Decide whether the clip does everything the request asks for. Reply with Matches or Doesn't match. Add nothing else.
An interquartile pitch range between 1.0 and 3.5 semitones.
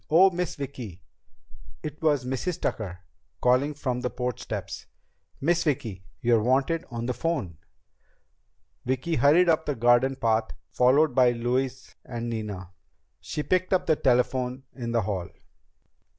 Doesn't match